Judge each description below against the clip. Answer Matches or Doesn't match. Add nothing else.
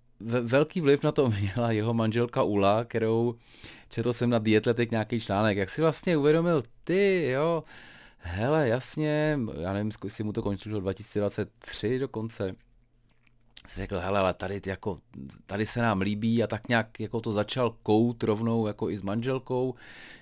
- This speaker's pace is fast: Doesn't match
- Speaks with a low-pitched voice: Matches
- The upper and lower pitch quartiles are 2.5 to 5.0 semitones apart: Matches